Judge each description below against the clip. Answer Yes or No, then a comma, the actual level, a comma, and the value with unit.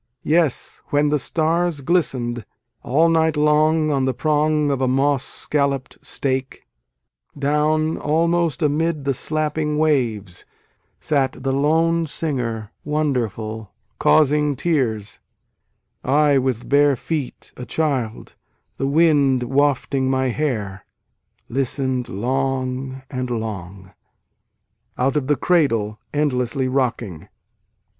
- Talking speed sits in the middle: No, slow, 115 wpm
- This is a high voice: No, medium, 140 Hz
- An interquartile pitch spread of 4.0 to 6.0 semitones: No, average, 3.2 semitones